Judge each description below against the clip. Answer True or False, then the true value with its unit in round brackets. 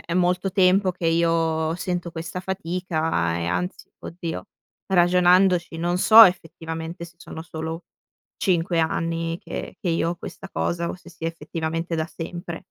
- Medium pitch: True (170 Hz)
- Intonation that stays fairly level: True (1.7 semitones)